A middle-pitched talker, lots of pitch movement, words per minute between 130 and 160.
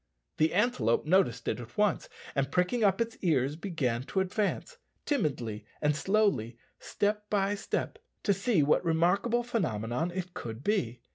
Yes: medium, 180 Hz; wide, 7.9 semitones; average, 150 wpm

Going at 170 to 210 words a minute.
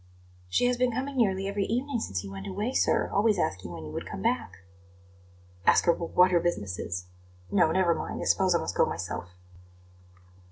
Yes: average, 200 wpm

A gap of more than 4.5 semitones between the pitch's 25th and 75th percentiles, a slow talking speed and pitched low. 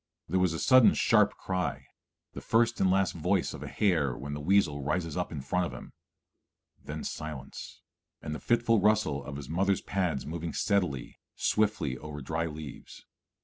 No: average, 4.9 semitones; average, 175 wpm; very low, 85 Hz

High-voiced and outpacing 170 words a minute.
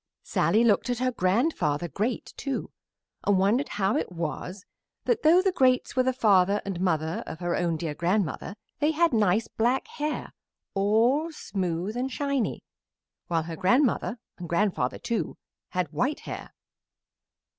No: high, 205 Hz; average, 150 wpm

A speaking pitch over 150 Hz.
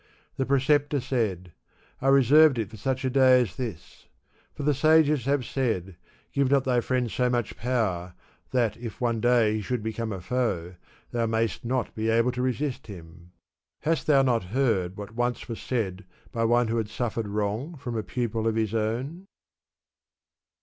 No: low, 120 Hz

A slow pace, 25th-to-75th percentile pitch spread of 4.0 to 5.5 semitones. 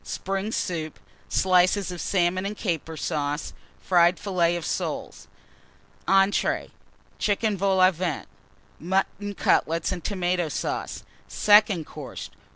No: slow, 110 wpm; narrow, 2.5 semitones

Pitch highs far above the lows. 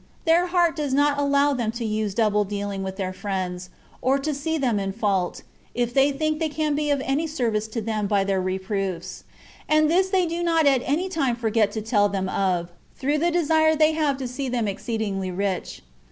Yes: wide, 7.0 semitones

